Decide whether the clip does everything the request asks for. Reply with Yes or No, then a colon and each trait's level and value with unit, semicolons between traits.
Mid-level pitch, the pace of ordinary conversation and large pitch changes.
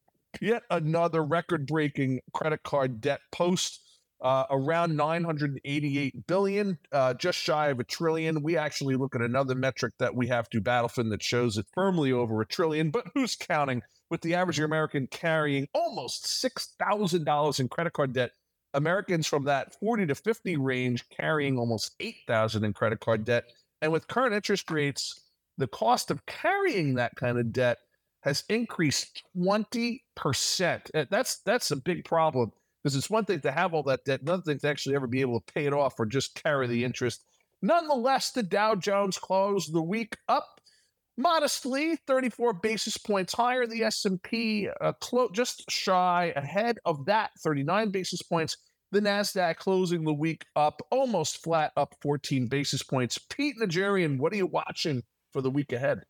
Yes: medium, 160 Hz; average, 170 wpm; wide, 7.1 semitones